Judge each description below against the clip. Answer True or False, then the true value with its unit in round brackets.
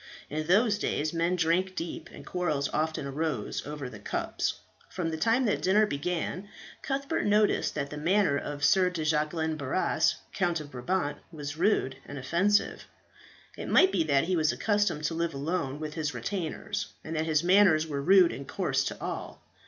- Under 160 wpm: False (185 wpm)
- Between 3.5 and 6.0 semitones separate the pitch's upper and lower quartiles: True (3.9 semitones)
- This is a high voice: False (160 Hz)